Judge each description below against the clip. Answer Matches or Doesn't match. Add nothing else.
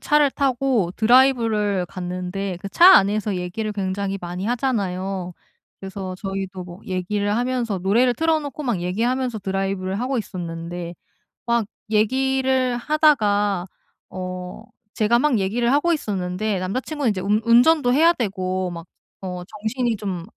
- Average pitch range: Matches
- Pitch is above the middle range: Matches